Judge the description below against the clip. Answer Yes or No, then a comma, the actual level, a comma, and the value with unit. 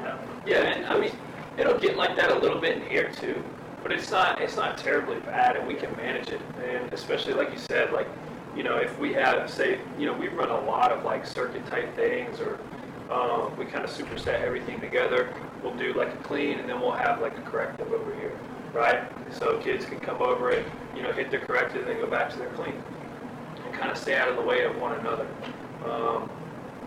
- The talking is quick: Yes, fast, 230 wpm